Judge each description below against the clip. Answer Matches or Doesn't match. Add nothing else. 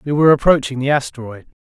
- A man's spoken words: Matches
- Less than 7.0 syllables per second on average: Doesn't match